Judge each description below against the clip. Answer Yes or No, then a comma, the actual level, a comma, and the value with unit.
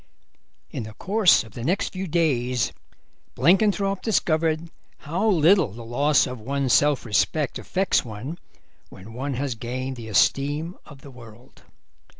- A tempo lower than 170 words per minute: Yes, average, 145 wpm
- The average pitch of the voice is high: No, medium, 140 Hz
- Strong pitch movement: Yes, wide, 5.8 semitones